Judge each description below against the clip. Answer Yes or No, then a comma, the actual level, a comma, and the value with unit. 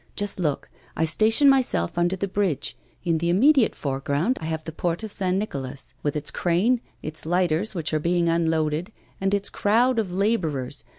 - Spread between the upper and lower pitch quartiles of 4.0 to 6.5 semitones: Yes, average, 4.6 semitones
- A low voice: No, medium, 175 Hz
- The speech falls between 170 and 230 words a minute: Yes, average, 180 wpm